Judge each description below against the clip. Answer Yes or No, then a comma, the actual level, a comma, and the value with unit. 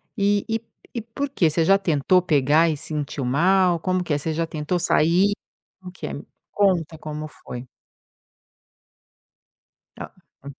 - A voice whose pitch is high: No, medium, 170 Hz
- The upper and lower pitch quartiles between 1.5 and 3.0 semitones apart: No, average, 4.1 semitones